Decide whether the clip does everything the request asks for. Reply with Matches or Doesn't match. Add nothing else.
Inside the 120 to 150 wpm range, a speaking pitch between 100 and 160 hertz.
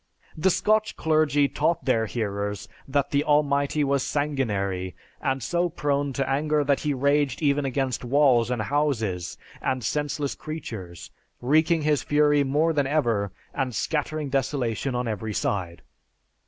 Matches